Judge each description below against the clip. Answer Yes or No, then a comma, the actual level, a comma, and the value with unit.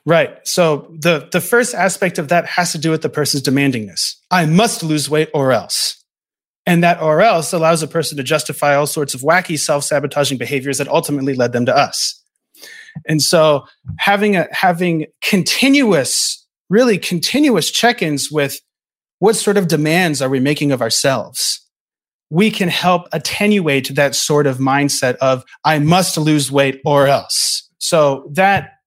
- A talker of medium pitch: Yes, medium, 155 Hz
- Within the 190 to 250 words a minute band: No, average, 160 wpm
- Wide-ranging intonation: No, average, 4.1 semitones